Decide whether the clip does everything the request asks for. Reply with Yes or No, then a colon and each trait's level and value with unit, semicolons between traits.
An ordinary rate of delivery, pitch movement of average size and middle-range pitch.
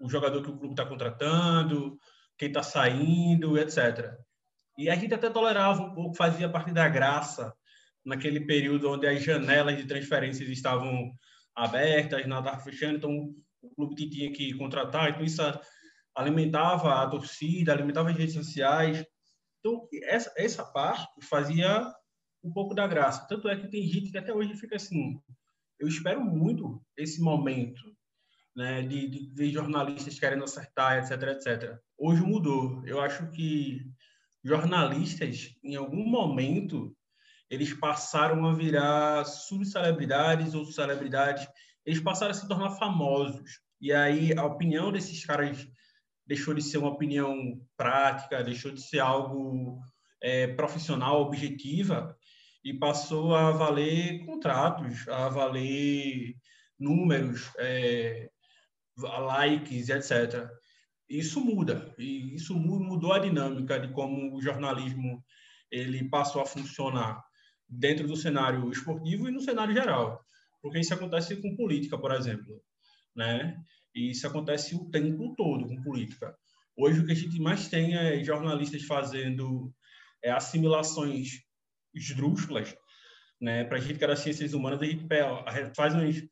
Yes: average, 135 wpm; average, 3.3 semitones; medium, 145 Hz